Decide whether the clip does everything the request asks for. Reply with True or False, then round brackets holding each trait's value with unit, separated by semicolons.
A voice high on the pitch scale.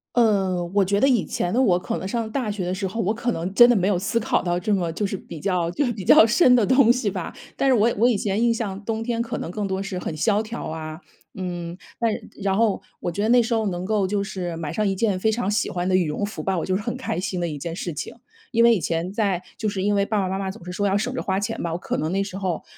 True (200 Hz)